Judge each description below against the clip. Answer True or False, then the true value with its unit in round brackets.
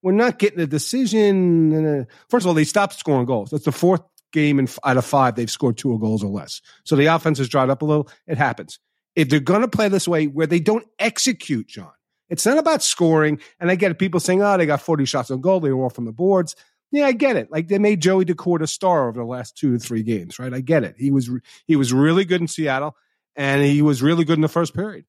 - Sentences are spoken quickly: True (260 wpm)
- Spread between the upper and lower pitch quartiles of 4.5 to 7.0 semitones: True (5.4 semitones)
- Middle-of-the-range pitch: True (155 Hz)